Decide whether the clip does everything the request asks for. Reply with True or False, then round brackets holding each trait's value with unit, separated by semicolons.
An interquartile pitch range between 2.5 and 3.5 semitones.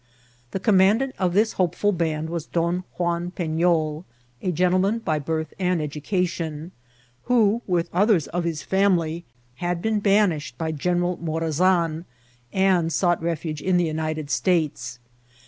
True (2.8 semitones)